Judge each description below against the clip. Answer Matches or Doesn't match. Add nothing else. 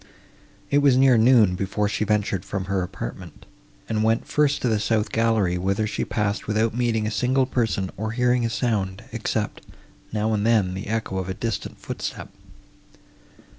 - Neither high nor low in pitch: Doesn't match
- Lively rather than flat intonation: Doesn't match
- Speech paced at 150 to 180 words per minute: Matches